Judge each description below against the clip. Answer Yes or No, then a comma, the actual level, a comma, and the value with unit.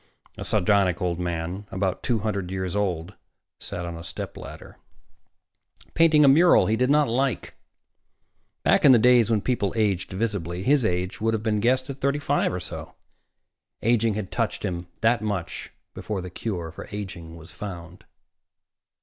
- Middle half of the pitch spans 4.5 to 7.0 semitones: Yes, average, 4.9 semitones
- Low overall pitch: Yes, low, 105 Hz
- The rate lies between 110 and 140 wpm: No, average, 165 wpm